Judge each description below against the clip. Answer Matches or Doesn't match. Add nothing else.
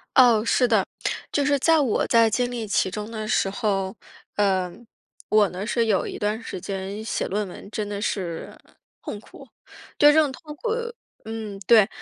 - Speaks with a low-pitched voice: Doesn't match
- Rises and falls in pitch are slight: Doesn't match